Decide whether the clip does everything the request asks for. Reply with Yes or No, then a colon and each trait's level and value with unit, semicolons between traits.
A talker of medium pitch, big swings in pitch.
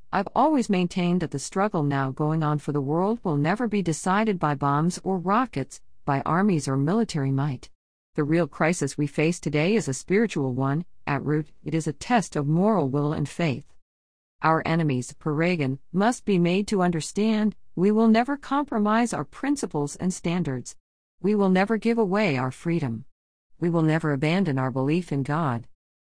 Yes: medium, 160 Hz; wide, 5.7 semitones